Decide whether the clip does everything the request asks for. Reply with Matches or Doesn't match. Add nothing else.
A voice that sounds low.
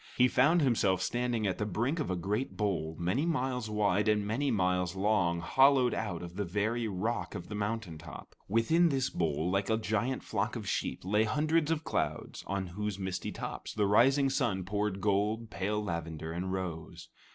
Matches